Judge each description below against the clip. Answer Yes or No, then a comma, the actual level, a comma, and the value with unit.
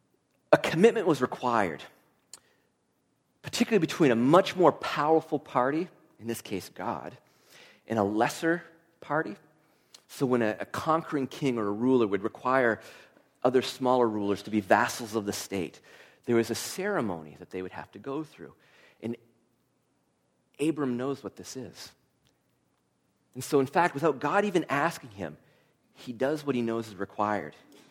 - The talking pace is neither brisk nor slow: Yes, average, 155 wpm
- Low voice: Yes, low, 125 Hz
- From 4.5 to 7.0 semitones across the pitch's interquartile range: Yes, average, 5.3 semitones